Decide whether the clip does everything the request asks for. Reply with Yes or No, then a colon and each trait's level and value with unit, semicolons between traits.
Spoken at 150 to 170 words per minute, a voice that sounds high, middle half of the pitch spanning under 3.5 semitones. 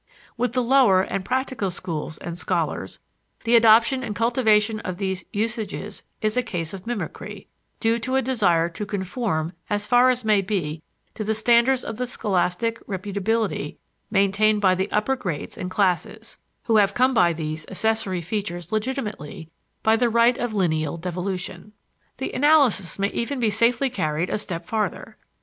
No: average, 160 wpm; high, 210 Hz; average, 4.2 semitones